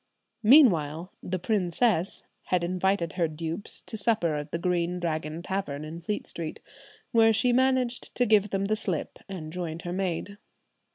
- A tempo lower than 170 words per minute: Yes, average, 160 wpm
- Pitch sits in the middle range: Yes, medium, 180 Hz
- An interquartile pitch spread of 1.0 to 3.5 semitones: No, average, 4.1 semitones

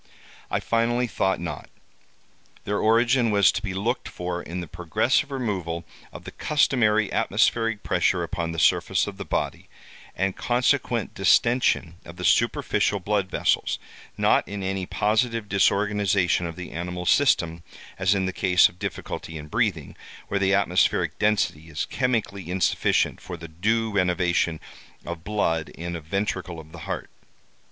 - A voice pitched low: Yes, very low, 95 Hz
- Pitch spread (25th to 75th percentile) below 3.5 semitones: No, average, 3.8 semitones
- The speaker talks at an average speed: Yes, average, 150 wpm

